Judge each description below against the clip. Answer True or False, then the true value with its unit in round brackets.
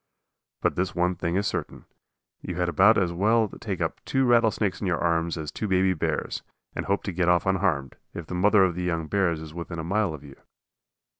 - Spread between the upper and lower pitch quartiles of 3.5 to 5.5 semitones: False (2.8 semitones)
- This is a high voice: False (90 Hz)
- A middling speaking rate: False (220 wpm)